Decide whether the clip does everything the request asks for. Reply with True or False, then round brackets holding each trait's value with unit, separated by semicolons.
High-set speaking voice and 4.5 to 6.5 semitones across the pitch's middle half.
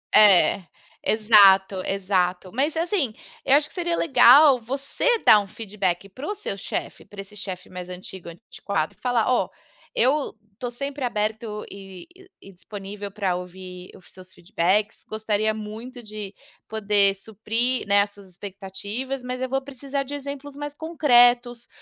True (215 Hz; 4.9 semitones)